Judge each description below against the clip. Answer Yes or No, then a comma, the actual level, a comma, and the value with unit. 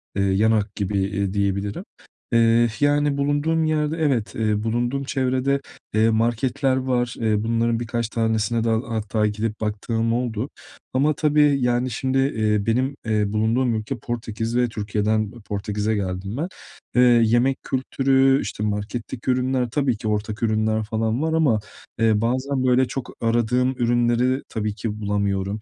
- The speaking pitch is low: Yes, low, 115 Hz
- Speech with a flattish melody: No, average, 3.3 semitones